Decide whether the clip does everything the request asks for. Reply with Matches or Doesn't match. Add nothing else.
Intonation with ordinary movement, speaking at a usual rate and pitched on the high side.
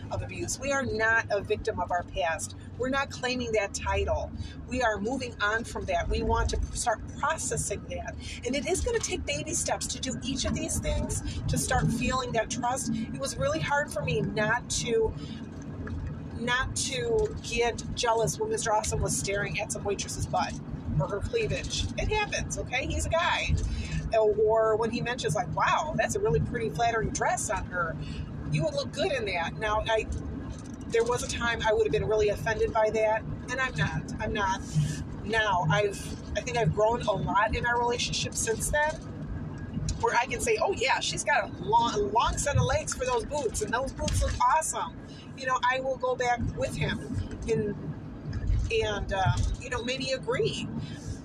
Matches